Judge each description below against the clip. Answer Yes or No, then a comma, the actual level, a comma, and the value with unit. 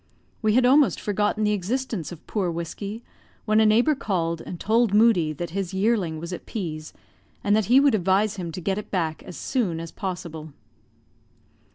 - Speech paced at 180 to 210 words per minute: Yes, average, 190 wpm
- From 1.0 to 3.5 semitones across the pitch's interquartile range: No, average, 4.3 semitones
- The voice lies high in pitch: Yes, high, 195 Hz